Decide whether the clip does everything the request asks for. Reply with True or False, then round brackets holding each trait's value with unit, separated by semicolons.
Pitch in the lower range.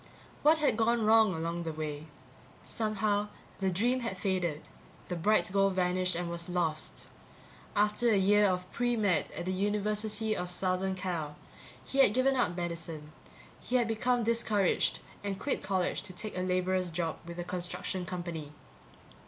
False (185 Hz)